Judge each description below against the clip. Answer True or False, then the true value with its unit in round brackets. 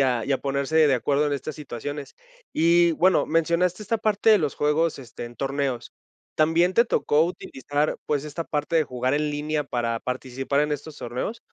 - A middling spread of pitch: True (3.4 semitones)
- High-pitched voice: False (150 Hz)